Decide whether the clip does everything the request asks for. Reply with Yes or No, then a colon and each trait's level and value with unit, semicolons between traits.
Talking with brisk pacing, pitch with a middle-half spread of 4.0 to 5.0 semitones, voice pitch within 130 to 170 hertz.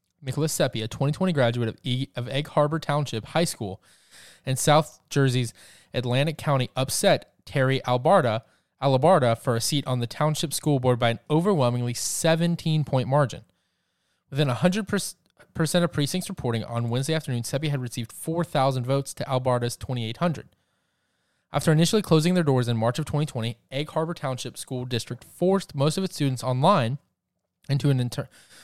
No: average, 160 wpm; average, 4.3 semitones; low, 135 Hz